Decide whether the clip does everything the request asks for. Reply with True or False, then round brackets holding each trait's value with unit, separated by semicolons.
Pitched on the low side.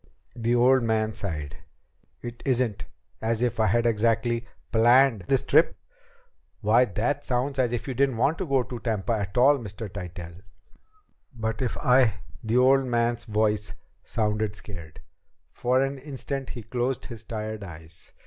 True (115 Hz)